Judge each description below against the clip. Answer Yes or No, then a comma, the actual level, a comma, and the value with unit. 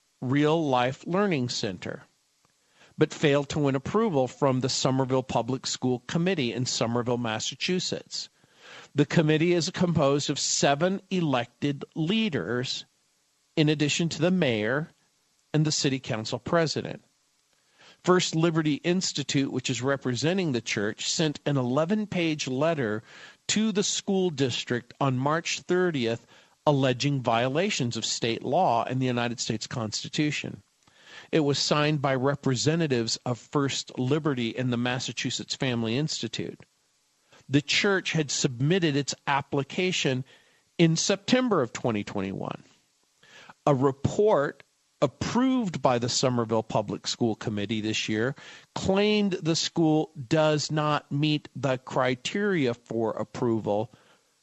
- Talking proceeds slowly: Yes, slow, 120 wpm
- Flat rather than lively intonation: No, average, 4.6 semitones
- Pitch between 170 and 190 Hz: No, medium, 140 Hz